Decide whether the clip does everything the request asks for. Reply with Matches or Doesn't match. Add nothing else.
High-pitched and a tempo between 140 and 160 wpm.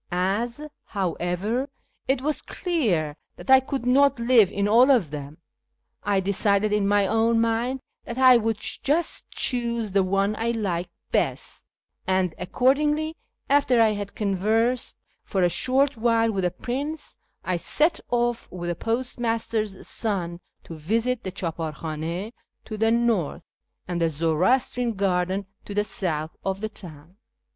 Matches